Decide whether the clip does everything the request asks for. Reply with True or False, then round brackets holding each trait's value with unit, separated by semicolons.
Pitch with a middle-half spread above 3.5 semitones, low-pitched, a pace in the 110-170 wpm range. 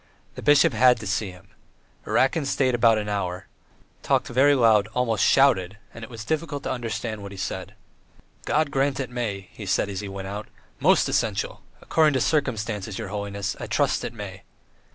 False (4.7 semitones; 115 Hz; 185 wpm)